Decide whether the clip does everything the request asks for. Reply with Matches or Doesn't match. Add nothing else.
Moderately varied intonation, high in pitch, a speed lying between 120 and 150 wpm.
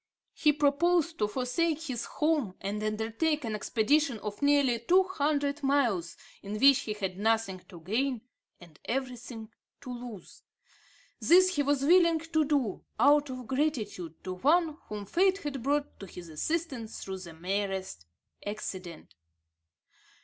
Doesn't match